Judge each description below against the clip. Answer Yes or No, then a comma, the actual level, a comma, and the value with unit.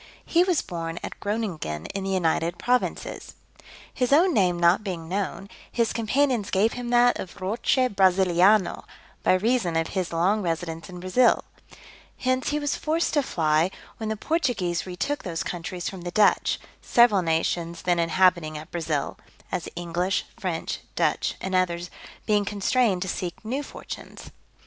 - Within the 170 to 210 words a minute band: No, average, 155 wpm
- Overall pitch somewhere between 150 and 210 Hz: Yes, high, 190 Hz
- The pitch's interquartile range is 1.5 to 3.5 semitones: No, average, 5.1 semitones